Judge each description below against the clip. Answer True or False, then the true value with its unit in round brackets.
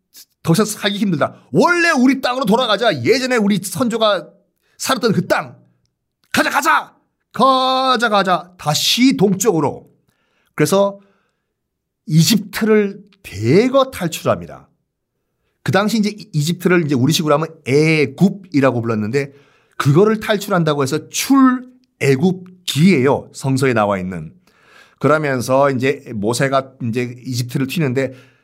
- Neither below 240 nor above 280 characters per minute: True (270 characters per minute)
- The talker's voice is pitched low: False (170 Hz)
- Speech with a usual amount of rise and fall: False (7.3 semitones)